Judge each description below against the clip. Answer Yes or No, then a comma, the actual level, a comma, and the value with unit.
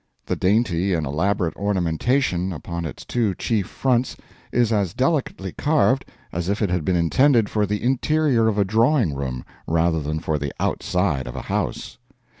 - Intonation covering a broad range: Yes, wide, 6.0 semitones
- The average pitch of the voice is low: Yes, very low, 95 Hz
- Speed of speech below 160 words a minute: No, average, 170 wpm